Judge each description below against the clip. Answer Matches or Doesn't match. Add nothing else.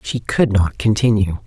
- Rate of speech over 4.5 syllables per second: Doesn't match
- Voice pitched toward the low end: Matches